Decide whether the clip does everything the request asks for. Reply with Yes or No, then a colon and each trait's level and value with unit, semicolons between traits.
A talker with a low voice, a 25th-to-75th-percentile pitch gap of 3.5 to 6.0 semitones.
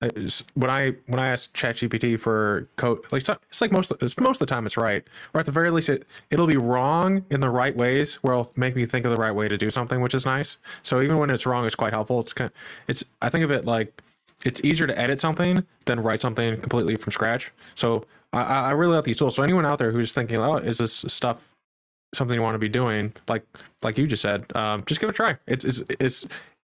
Yes: low, 125 Hz; average, 3.8 semitones